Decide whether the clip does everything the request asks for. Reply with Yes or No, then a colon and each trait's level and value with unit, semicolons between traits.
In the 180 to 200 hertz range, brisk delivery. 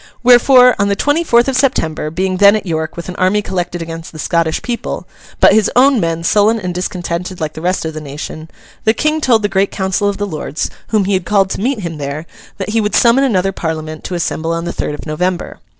Yes: medium, 185 Hz; fast, 235 wpm